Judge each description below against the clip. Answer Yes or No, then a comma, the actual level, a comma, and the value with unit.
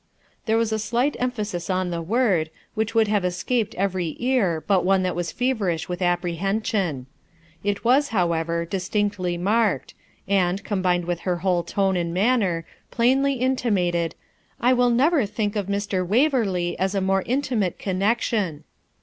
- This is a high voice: Yes, high, 195 Hz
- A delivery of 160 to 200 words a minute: No, average, 150 wpm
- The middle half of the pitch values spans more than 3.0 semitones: Yes, average, 4.4 semitones